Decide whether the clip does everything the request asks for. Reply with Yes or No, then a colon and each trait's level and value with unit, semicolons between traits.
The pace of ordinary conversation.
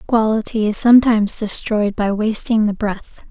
Yes: average, 165 wpm